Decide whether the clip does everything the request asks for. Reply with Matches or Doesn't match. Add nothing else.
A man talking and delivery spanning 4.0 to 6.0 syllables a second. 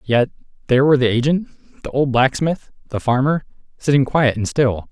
Matches